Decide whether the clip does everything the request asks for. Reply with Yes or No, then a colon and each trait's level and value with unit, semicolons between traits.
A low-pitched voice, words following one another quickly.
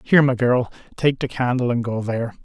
Yes: low, 125 Hz; fast, 220 wpm